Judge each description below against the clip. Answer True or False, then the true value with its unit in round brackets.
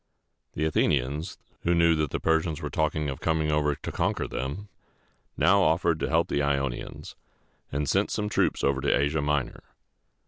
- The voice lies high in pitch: False (75 Hz)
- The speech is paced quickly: False (170 wpm)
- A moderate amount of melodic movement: False (2.3 semitones)